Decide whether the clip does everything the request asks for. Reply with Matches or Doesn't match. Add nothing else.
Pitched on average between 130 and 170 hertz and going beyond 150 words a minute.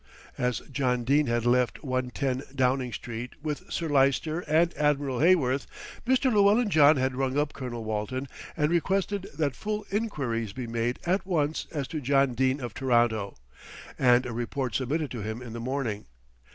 Matches